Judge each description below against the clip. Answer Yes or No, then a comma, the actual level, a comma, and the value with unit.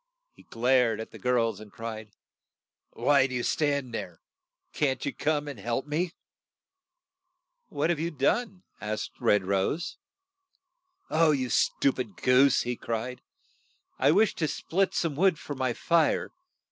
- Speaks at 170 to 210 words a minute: No, average, 150 wpm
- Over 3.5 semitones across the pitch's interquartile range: Yes, average, 5.1 semitones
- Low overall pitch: Yes, low, 130 Hz